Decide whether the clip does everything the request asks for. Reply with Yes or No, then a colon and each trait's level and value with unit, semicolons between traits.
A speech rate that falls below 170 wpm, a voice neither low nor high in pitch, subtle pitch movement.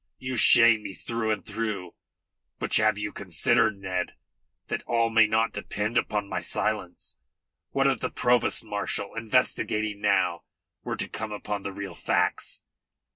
No: average, 150 wpm; low, 105 Hz; narrow, 2.1 semitones